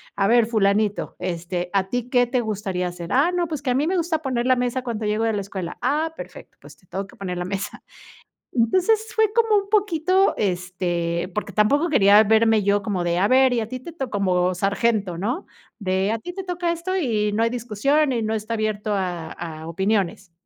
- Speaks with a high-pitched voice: Yes, high, 220 Hz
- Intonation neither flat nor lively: No, wide, 5.7 semitones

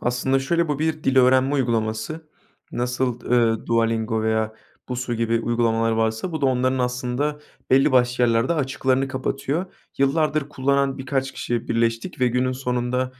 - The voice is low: Yes, low, 125 Hz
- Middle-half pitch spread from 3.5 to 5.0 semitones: No, narrow, 2.6 semitones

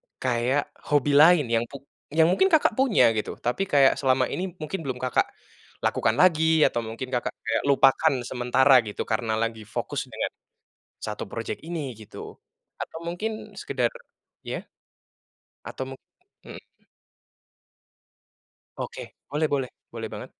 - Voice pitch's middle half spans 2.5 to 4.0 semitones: No, average, 4.8 semitones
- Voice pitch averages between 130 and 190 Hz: Yes, low, 135 Hz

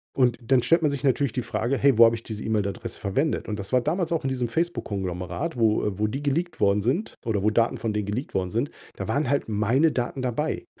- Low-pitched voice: Yes, low, 120 Hz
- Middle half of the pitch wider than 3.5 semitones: Yes, average, 5.1 semitones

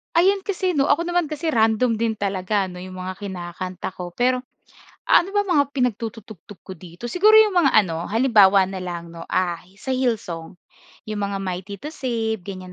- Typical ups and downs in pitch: No, wide, 6.7 semitones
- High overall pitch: Yes, high, 215 Hz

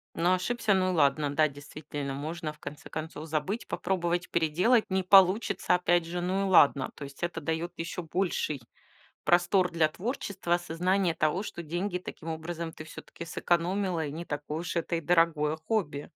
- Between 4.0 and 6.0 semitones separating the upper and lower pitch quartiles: No, average, 2.9 semitones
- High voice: No, medium, 170 Hz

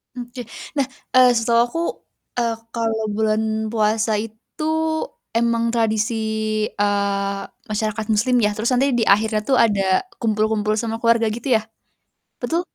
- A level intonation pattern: Yes, narrow, 1.8 semitones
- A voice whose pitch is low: No, high, 225 Hz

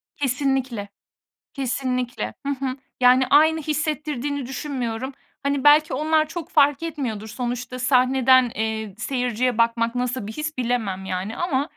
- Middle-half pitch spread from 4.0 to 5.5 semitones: No, average, 3.3 semitones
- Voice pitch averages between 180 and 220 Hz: No, very high, 255 Hz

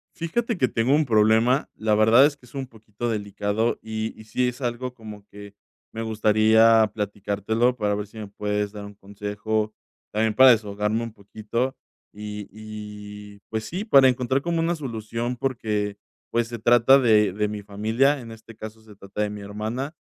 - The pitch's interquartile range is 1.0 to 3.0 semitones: Yes, average, 2.7 semitones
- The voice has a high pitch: No, low, 110 Hz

